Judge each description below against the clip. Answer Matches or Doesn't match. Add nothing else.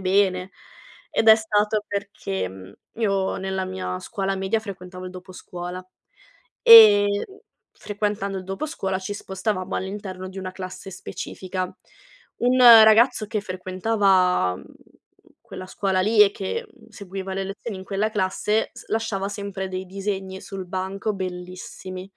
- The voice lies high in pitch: Matches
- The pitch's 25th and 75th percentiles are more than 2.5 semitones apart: Doesn't match